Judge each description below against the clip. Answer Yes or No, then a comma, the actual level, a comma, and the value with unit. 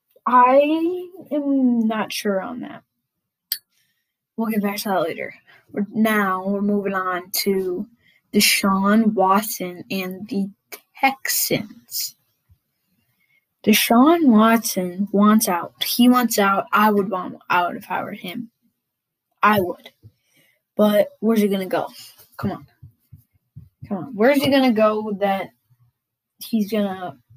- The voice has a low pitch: No, high, 205 Hz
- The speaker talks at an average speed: No, slow, 125 wpm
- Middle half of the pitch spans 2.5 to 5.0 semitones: Yes, average, 3.9 semitones